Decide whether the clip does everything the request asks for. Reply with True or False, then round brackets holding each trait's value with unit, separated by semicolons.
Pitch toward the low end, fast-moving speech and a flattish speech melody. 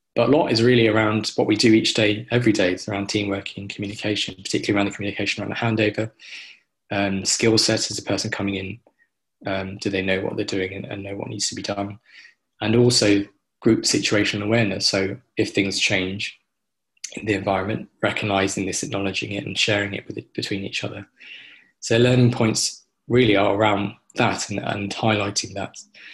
False (100 Hz; 190 wpm; 1.8 semitones)